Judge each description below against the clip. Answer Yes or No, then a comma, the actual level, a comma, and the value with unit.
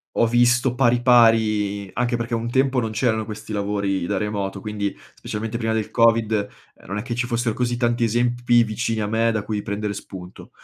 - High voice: No, low, 115 Hz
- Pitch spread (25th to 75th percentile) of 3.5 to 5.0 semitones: No, narrow, 2.4 semitones